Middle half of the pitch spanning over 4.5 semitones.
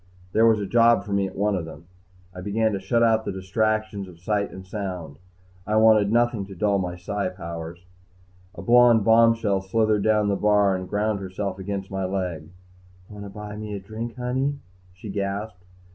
No: narrow, 2.6 semitones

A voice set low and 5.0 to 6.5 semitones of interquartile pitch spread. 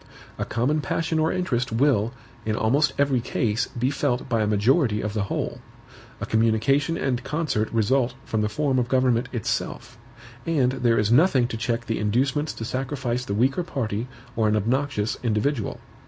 No: low, 125 Hz; average, 3.8 semitones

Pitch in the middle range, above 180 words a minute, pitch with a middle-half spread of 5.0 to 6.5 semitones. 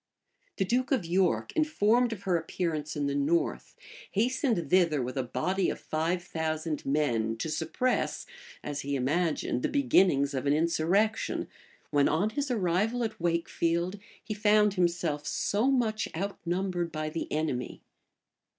No: medium, 170 Hz; average, 145 wpm; wide, 5.4 semitones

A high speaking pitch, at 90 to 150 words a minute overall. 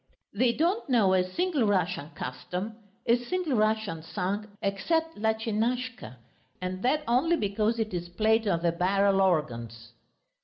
Yes: high, 210 Hz; average, 140 wpm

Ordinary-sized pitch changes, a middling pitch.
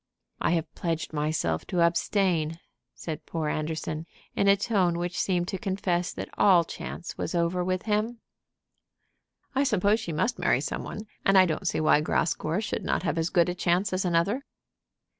Yes: average, 3.1 semitones; medium, 175 Hz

